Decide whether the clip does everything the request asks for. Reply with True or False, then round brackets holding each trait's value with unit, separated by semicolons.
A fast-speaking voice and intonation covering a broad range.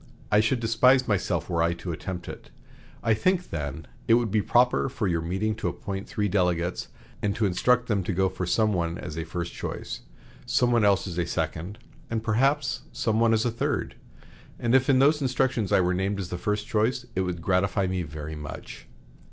False (210 wpm; 4.8 semitones)